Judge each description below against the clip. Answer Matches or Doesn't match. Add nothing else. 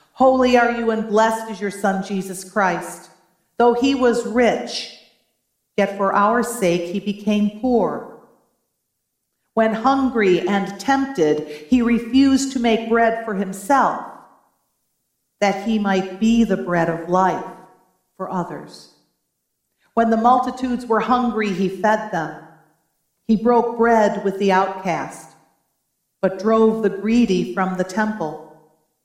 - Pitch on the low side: Doesn't match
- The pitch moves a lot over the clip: Doesn't match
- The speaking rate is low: Matches